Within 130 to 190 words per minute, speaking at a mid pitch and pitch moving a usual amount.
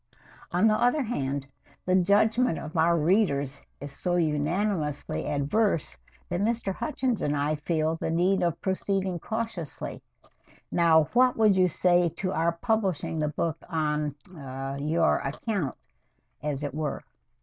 Yes: average, 145 wpm; medium, 170 Hz; average, 4.9 semitones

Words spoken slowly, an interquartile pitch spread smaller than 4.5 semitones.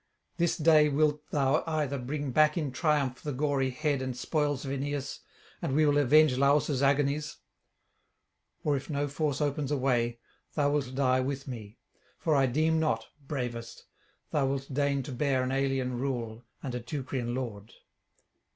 No: average, 165 wpm; narrow, 2.5 semitones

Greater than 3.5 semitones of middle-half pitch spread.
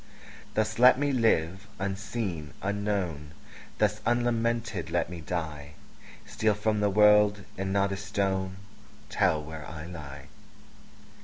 Yes: average, 4.3 semitones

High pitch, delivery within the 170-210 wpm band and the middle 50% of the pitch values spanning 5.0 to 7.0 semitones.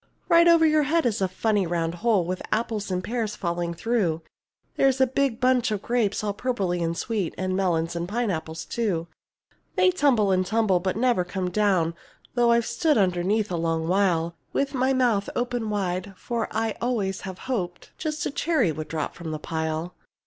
Yes: high, 205 Hz; average, 185 wpm; wide, 5.5 semitones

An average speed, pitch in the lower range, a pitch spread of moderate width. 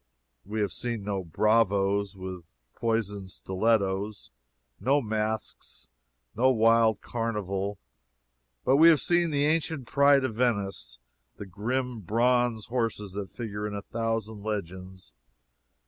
No: slow, 120 wpm; low, 110 Hz; average, 3.3 semitones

